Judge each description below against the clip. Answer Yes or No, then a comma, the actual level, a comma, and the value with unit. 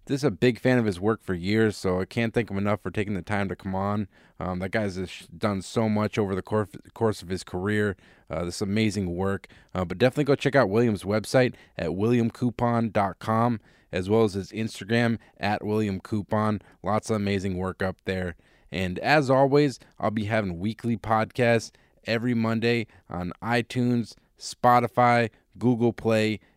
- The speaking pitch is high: No, low, 110 Hz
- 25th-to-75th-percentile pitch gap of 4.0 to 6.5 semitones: No, average, 3.5 semitones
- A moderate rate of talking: Yes, average, 175 wpm